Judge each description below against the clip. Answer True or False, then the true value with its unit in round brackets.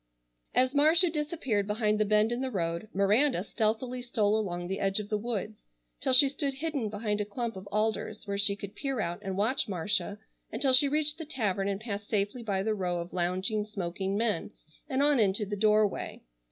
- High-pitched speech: True (215 Hz)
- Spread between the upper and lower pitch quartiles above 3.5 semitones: True (4.1 semitones)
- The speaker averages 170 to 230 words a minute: True (200 wpm)